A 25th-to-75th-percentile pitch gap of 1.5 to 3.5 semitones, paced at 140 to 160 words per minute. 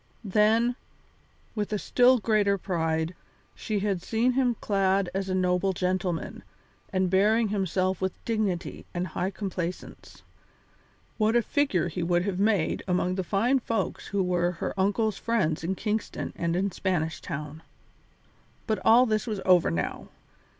Yes: average, 3.2 semitones; average, 150 wpm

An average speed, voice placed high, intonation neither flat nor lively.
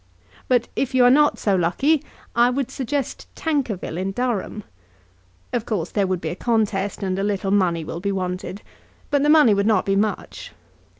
Yes: average, 185 wpm; high, 210 Hz; average, 4.7 semitones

